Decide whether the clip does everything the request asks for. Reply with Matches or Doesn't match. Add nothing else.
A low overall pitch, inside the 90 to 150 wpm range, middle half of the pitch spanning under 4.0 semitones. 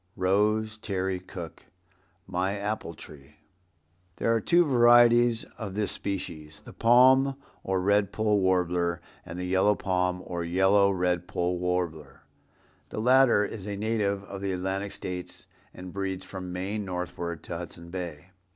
Matches